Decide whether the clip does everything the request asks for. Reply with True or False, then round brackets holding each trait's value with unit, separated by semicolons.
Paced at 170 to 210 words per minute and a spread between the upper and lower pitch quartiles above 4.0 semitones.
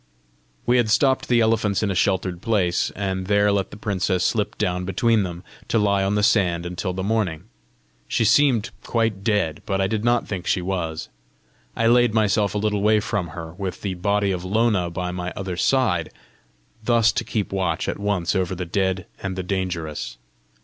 False (190 wpm; 3.0 semitones)